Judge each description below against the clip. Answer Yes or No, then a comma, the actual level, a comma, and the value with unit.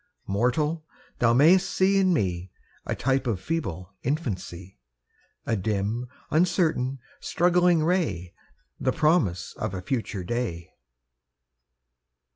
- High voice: No, low, 125 Hz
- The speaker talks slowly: Yes, slow, 105 wpm